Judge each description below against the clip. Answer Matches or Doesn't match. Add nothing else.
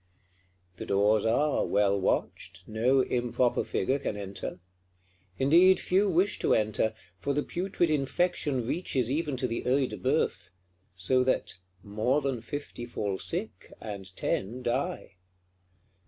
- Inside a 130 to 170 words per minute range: Matches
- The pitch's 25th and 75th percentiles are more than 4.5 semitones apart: Matches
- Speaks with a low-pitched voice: Matches